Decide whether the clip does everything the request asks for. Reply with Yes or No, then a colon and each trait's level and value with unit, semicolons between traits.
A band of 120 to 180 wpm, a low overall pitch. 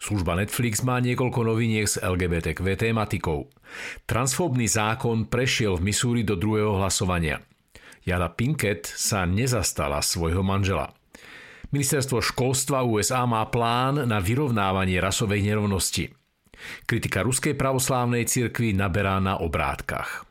No: slow, 110 wpm; low, 110 Hz